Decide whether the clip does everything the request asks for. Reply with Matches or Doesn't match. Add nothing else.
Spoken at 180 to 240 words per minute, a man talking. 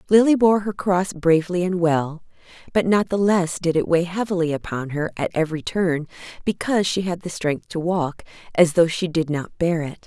Doesn't match